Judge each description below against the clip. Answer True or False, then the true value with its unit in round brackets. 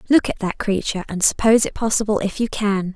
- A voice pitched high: True (210 Hz)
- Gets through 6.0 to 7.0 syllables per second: True (6.3 syllables/s)